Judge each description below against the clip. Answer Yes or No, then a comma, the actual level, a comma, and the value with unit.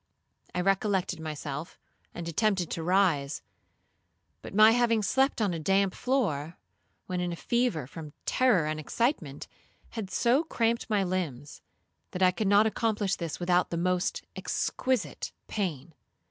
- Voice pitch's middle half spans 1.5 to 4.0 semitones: No, average, 5.0 semitones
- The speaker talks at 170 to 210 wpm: No, average, 145 wpm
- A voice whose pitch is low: No, medium, 185 Hz